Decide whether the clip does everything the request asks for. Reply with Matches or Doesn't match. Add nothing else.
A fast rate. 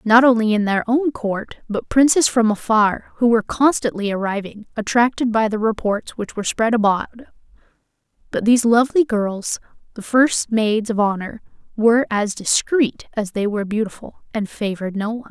Doesn't match